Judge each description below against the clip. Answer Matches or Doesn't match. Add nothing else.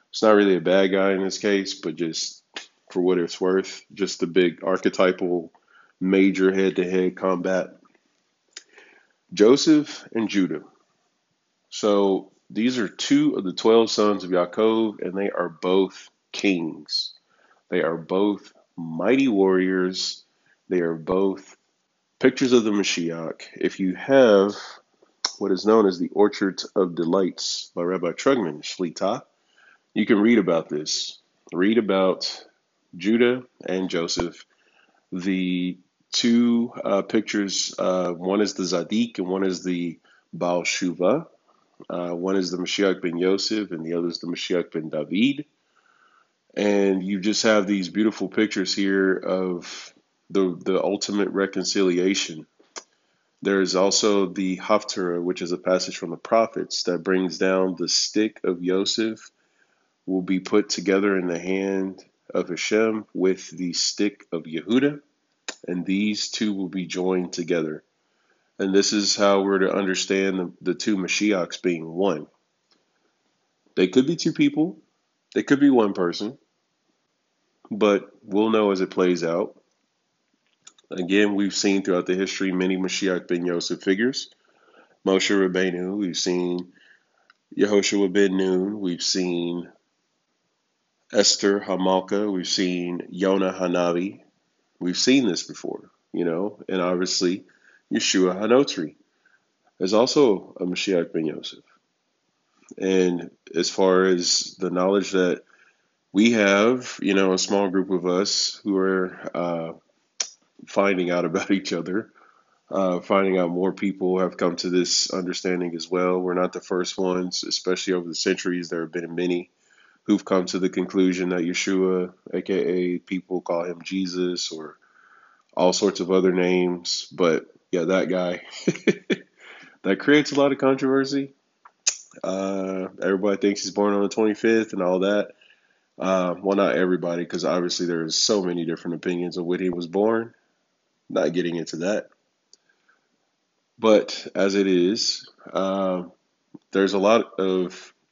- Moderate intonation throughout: Doesn't match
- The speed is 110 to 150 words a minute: Matches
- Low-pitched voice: Matches